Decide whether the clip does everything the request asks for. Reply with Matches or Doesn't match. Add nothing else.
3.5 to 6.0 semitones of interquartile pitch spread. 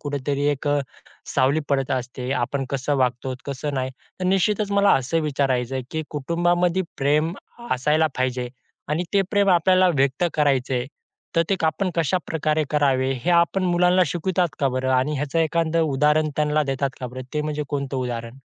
Matches